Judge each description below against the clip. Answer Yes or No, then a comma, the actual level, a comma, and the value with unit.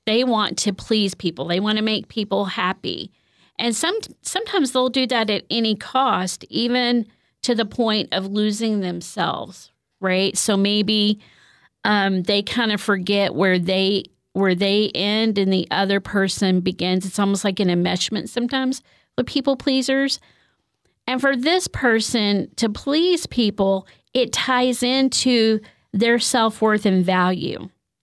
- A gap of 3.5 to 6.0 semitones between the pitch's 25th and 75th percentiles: Yes, average, 3.8 semitones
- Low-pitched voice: No, high, 210 Hz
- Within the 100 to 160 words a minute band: Yes, average, 150 wpm